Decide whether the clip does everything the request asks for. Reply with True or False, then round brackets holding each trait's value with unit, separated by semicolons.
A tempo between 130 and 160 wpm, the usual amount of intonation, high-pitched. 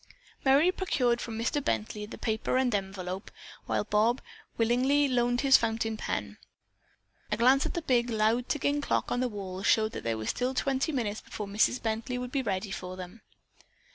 False (180 wpm; 3.7 semitones; 230 Hz)